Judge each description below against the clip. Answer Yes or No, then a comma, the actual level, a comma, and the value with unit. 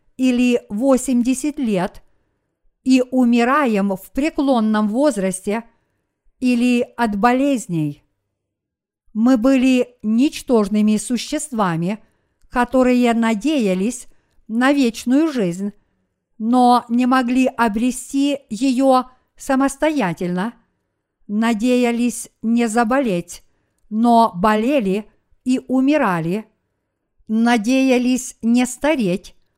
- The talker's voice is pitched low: No, high, 240 Hz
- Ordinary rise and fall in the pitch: Yes, average, 3.5 semitones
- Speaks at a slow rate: Yes, slow, 75 wpm